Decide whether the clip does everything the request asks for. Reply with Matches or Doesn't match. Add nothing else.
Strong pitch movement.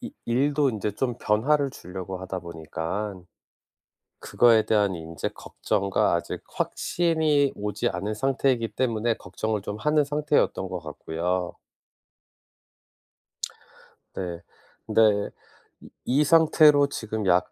Matches